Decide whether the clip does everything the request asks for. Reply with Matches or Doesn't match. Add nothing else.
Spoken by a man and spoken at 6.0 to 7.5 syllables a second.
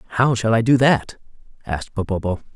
Matches